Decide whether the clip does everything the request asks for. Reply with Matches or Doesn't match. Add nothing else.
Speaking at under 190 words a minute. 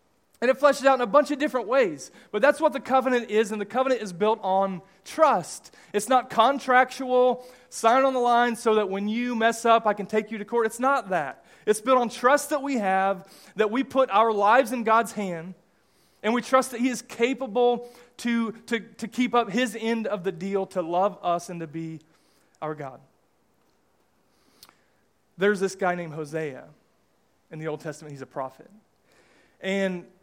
Doesn't match